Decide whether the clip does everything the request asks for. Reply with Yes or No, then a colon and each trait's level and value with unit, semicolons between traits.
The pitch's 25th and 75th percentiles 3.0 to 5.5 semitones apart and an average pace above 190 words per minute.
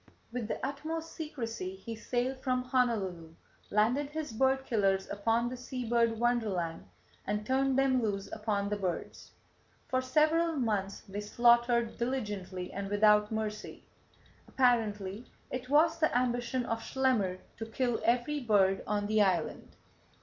No: average, 3.9 semitones; average, 140 wpm